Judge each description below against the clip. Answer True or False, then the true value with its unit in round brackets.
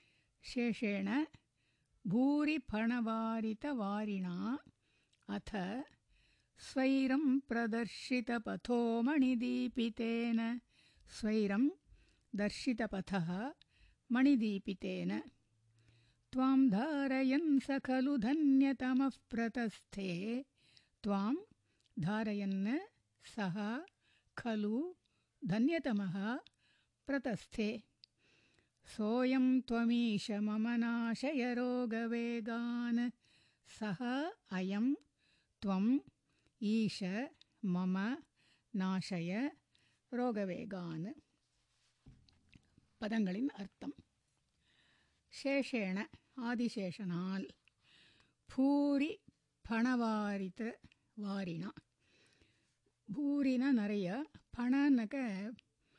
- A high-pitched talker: True (235 Hz)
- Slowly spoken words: True (40 wpm)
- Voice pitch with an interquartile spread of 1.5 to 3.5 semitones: False (4.5 semitones)